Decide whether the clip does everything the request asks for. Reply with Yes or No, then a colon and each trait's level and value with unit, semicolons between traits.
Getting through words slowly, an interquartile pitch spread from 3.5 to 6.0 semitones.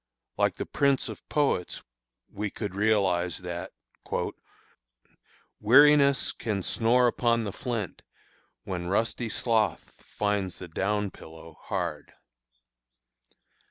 Yes: slow, 100 wpm; average, 4.2 semitones